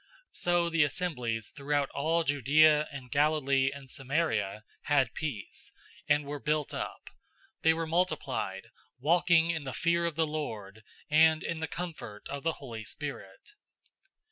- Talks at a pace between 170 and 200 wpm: No, average, 145 wpm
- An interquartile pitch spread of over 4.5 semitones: No, average, 3.4 semitones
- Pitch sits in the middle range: Yes, medium, 150 Hz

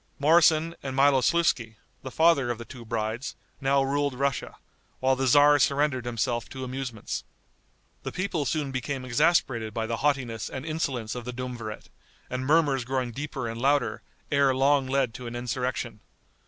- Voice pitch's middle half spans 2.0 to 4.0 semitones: Yes, average, 2.8 semitones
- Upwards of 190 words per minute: No, average, 160 wpm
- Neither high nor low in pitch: No, low, 130 Hz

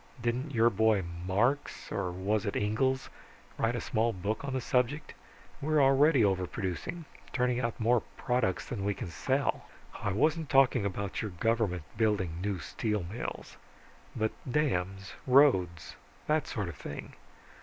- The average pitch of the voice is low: Yes, low, 110 Hz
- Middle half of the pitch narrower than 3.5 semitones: No, average, 5.3 semitones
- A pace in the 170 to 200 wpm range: No, average, 145 wpm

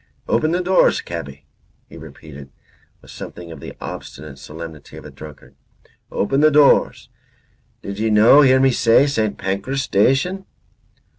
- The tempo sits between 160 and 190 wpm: No, average, 145 wpm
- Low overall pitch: Yes, low, 110 Hz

